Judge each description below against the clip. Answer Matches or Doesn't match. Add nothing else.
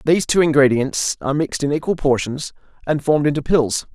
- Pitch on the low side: Doesn't match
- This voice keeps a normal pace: Matches